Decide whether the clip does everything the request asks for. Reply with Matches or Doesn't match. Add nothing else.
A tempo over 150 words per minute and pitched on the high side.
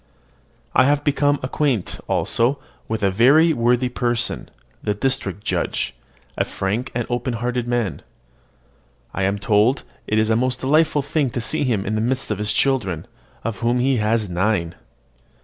Doesn't match